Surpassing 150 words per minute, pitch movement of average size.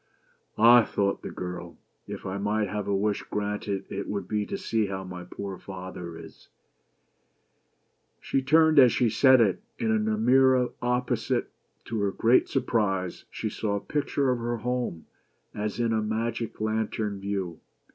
Yes: average, 175 wpm; average, 3.7 semitones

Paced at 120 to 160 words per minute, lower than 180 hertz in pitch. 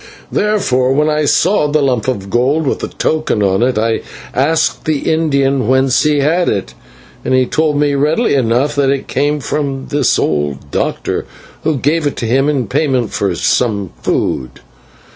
No: average, 175 wpm; low, 135 Hz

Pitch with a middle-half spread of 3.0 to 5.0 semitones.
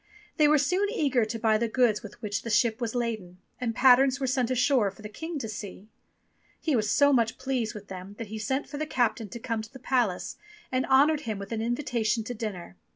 Yes: average, 3.6 semitones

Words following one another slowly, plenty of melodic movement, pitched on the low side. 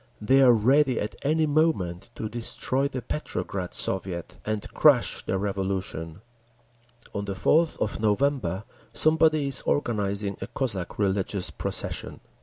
Yes: slow, 130 wpm; wide, 6.1 semitones; low, 105 Hz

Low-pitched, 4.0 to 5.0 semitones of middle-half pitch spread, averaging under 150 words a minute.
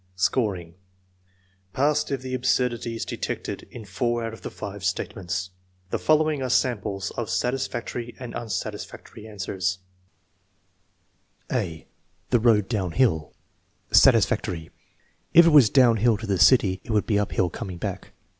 Yes: low, 110 Hz; average, 4.6 semitones; slow, 135 wpm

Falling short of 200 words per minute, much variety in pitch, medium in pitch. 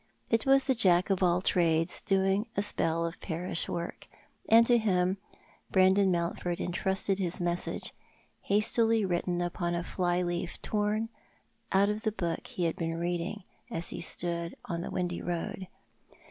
No: average, 160 wpm; narrow, 2.6 semitones; medium, 180 Hz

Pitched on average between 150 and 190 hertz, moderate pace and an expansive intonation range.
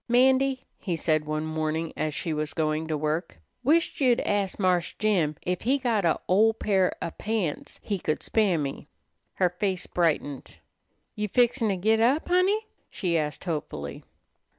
Yes: medium, 185 Hz; average, 165 wpm; wide, 6.3 semitones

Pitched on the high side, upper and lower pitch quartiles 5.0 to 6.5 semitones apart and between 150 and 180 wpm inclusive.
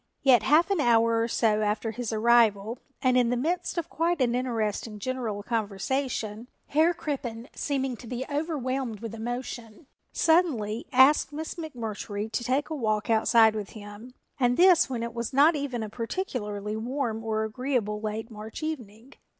No: high, 235 Hz; average, 3.8 semitones; average, 165 wpm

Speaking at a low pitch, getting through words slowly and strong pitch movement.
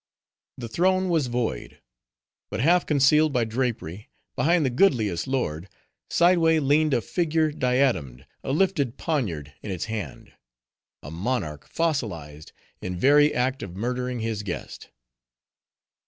Yes: low, 125 Hz; slow, 125 wpm; wide, 7.9 semitones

